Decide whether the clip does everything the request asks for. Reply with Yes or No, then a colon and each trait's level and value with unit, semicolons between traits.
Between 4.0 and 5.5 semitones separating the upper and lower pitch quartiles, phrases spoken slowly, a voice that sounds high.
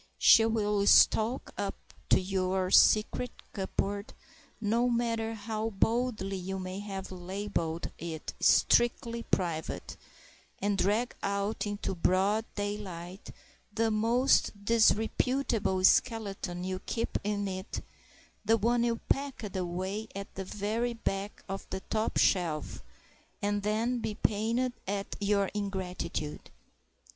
No: average, 2.9 semitones; slow, 115 wpm; high, 205 Hz